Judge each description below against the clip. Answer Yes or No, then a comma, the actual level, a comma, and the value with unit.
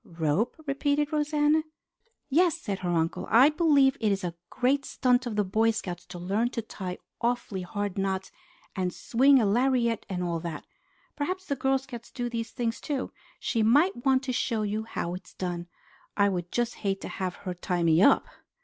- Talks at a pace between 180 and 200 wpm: Yes, average, 195 wpm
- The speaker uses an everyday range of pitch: No, wide, 6.2 semitones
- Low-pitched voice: No, high, 225 Hz